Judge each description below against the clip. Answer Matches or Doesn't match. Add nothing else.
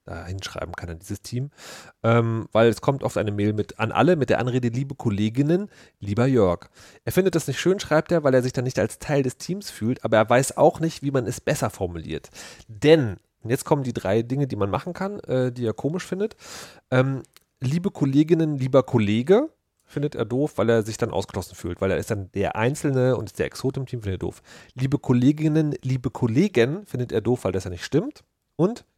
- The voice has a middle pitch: Doesn't match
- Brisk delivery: Matches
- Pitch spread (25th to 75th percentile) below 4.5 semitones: Doesn't match